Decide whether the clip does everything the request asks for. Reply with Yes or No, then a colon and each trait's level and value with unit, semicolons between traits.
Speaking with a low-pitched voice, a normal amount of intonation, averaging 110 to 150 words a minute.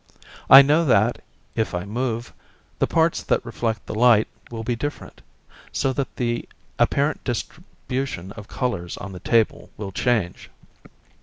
Yes: low, 120 Hz; average, 3.8 semitones; average, 145 wpm